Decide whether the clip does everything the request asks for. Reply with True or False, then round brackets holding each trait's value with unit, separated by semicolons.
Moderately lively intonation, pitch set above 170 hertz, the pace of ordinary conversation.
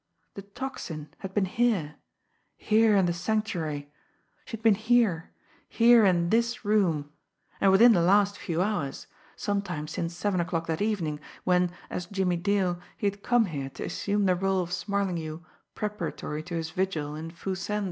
True (3.7 semitones; 185 Hz; 165 wpm)